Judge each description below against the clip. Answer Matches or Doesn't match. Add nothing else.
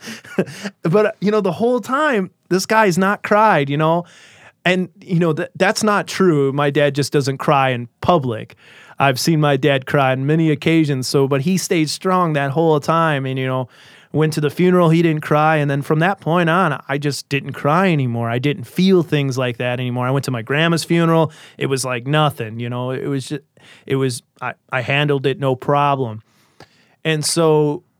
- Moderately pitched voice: Matches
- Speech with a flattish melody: Doesn't match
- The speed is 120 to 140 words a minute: Doesn't match